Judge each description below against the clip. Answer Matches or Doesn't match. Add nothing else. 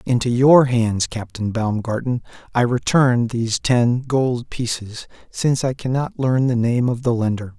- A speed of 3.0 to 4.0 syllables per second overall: Doesn't match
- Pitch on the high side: Doesn't match